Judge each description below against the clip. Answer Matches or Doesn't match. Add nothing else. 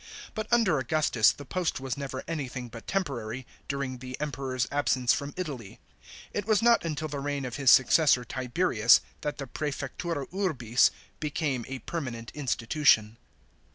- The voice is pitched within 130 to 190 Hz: Matches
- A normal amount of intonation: Matches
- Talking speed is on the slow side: Doesn't match